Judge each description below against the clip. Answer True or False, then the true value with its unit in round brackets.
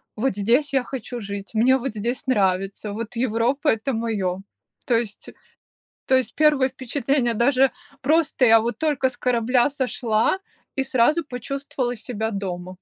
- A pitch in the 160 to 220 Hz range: False (245 Hz)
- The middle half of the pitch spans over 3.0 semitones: True (3.4 semitones)